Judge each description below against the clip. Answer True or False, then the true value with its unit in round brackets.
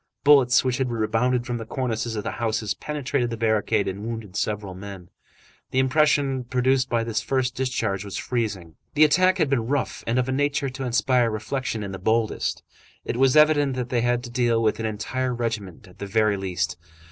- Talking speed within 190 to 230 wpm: True (200 wpm)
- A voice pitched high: False (120 Hz)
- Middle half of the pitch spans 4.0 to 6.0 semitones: False (3.3 semitones)